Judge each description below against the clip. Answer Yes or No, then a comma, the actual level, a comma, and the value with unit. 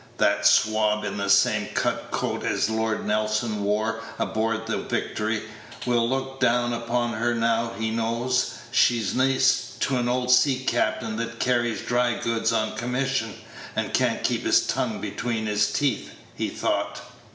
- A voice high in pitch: No, low, 115 Hz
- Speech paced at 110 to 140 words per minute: No, average, 155 wpm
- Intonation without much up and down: Yes, narrow, 2.1 semitones